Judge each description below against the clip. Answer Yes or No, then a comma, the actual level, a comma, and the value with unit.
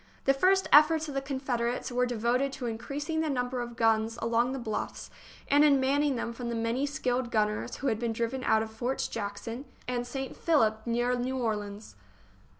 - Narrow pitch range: No, average, 3.0 semitones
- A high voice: Yes, high, 245 Hz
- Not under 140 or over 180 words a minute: No, average, 195 wpm